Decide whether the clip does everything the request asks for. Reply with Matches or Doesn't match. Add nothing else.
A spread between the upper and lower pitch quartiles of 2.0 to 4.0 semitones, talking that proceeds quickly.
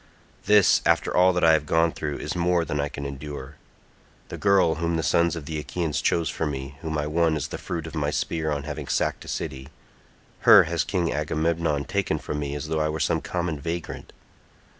Matches